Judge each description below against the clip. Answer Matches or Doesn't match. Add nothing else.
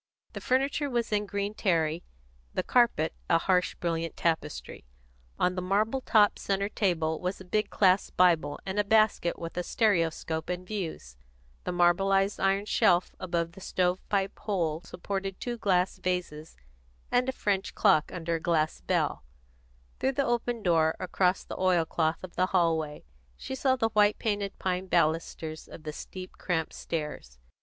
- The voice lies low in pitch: Doesn't match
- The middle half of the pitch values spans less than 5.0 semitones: Matches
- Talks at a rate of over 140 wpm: Matches